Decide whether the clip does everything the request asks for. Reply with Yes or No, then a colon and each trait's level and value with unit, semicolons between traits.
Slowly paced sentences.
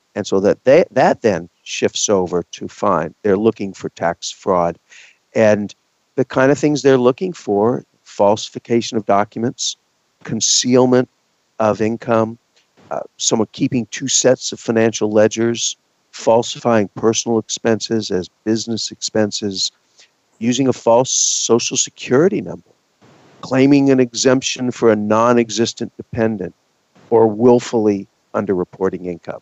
Yes: slow, 120 wpm